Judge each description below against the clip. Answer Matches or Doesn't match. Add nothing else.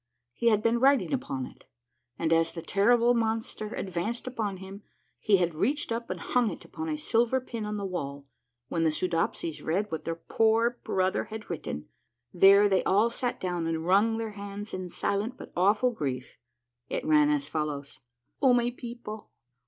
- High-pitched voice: Matches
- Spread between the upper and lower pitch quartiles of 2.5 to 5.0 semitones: Doesn't match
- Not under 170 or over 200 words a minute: Matches